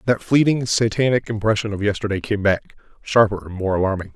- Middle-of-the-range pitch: No, low, 105 Hz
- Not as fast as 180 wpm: Yes, average, 160 wpm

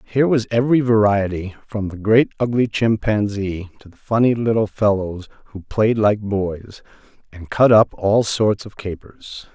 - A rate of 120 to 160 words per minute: Yes, average, 155 wpm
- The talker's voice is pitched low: Yes, low, 105 Hz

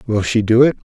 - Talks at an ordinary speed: No, fast, 265 wpm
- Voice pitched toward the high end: No, low, 115 Hz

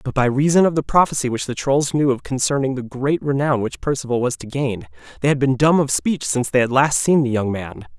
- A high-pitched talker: No, low, 135 Hz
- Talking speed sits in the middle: No, fast, 255 wpm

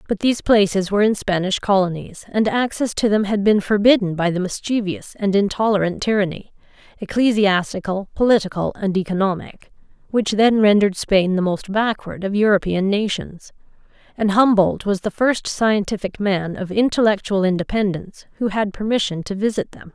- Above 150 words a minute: No, average, 145 wpm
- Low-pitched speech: No, high, 200 Hz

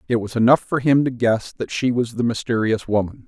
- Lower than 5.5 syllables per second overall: No, 5.6 syllables/s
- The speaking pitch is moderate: No, low, 120 Hz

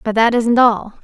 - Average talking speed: No, fast, 235 wpm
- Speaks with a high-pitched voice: Yes, high, 230 Hz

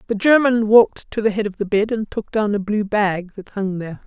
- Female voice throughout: Yes, female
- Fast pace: Yes, fast, 265 wpm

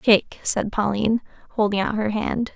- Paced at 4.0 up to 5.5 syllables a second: Yes, 5.3 syllables/s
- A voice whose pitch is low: No, high, 210 Hz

